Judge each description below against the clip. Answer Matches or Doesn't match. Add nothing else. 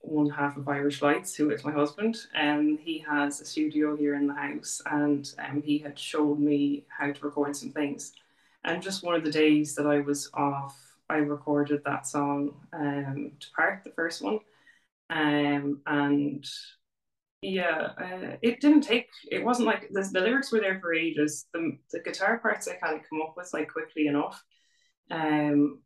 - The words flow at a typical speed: Matches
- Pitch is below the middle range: Doesn't match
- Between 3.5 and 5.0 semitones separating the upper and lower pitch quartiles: Doesn't match